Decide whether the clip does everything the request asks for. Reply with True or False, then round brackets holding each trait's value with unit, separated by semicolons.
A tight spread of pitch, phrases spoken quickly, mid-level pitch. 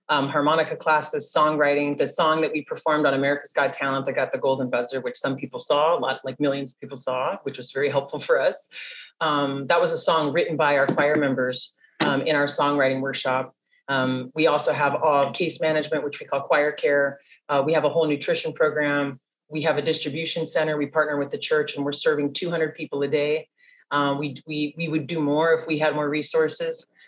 True (2.0 semitones; 215 wpm; 145 Hz)